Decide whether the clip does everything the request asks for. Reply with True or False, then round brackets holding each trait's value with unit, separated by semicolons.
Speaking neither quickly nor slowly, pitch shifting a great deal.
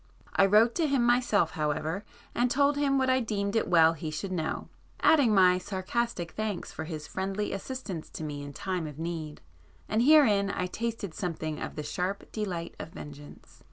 True (180 wpm; 6.3 semitones)